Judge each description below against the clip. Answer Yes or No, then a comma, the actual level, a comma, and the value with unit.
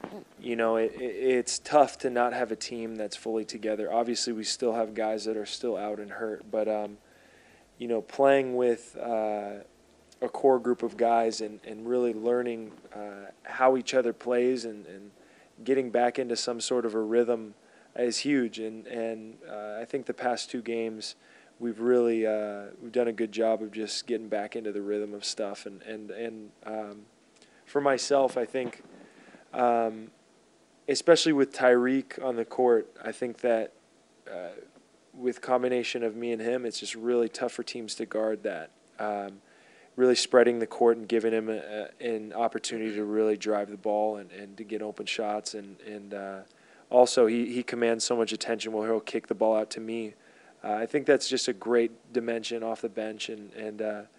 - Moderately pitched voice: No, low, 115 Hz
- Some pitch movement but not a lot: No, narrow, 2.2 semitones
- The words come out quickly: No, average, 190 wpm